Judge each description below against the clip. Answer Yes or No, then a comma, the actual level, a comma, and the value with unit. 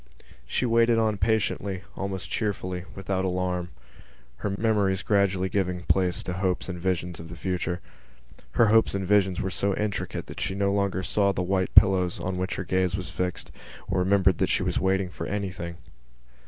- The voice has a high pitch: No, very low, 95 Hz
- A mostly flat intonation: Yes, narrow, 1.6 semitones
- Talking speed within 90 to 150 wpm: No, average, 180 wpm